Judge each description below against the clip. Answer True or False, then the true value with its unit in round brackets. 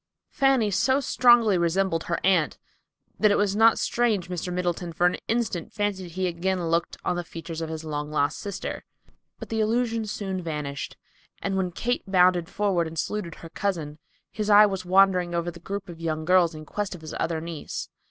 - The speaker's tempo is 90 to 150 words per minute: False (190 wpm)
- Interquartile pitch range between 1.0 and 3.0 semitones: False (3.6 semitones)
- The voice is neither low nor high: True (180 Hz)